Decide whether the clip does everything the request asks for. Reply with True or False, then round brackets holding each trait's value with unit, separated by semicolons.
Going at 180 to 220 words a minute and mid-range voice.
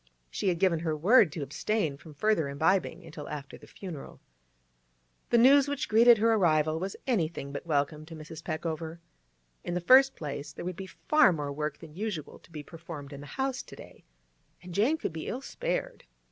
True (195 wpm; 165 Hz)